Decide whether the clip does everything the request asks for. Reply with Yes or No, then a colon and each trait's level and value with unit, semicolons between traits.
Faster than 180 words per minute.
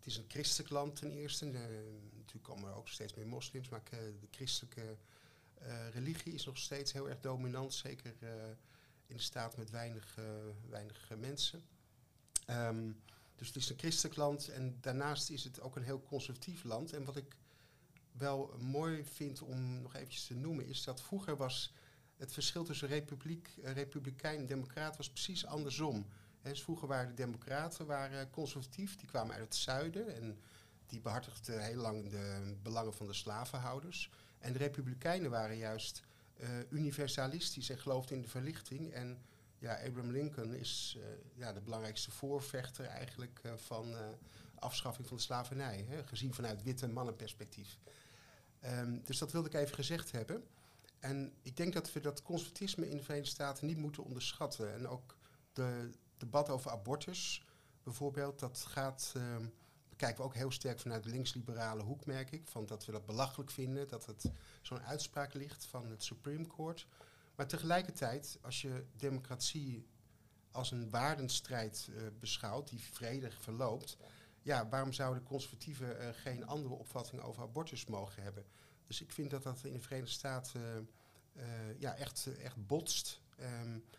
No: average, 170 wpm